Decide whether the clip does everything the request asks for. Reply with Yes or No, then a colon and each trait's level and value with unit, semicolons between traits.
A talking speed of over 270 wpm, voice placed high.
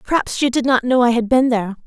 Yes: fast, 290 wpm; high, 245 Hz